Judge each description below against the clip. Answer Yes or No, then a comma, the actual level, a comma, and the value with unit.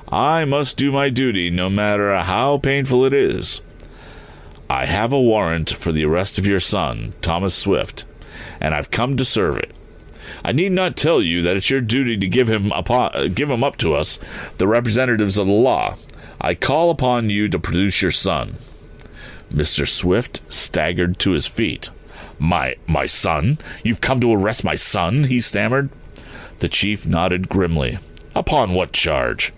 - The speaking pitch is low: Yes, low, 105 Hz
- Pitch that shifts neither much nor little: No, wide, 6.2 semitones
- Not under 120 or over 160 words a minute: No, average, 170 wpm